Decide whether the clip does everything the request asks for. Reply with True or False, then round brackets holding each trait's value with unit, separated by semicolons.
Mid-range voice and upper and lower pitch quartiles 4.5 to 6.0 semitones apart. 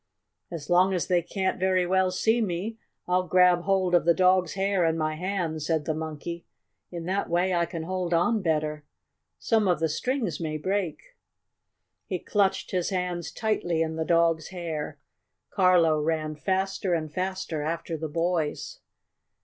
False (175 Hz; 2.7 semitones)